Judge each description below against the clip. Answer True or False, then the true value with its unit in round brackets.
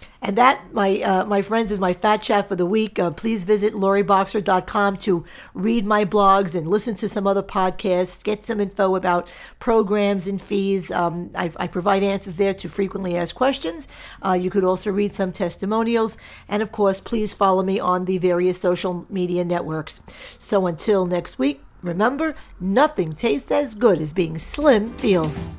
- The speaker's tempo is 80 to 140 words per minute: False (180 wpm)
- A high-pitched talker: True (195 Hz)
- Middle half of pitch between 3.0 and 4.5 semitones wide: False (2.6 semitones)